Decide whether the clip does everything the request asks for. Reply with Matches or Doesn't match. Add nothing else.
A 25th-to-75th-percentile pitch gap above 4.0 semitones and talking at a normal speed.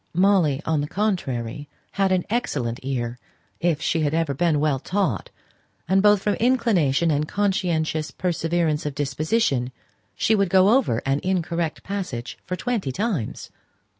Matches